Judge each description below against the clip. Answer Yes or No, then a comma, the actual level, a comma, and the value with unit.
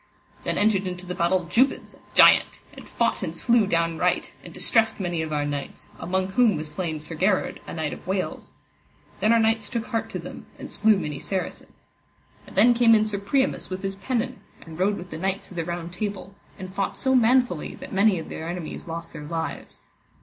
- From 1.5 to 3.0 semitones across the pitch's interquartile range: No, average, 4.6 semitones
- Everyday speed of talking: No, fast, 210 wpm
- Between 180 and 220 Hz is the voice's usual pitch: Yes, high, 190 Hz